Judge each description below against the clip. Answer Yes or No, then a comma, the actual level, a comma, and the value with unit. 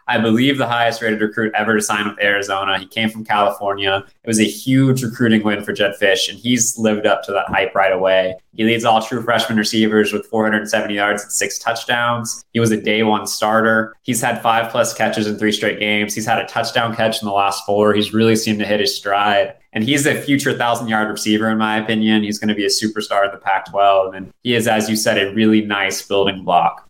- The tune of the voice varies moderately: No, narrow, 1.8 semitones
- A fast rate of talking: Yes, fast, 240 wpm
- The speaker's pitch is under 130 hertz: Yes, low, 110 Hz